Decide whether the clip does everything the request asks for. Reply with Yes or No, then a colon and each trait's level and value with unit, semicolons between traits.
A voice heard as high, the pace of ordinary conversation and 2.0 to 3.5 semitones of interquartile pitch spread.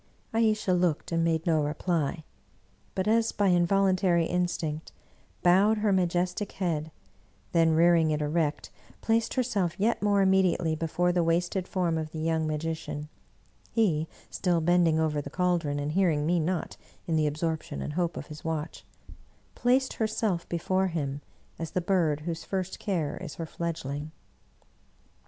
No: medium, 170 Hz; average, 155 wpm; average, 3.0 semitones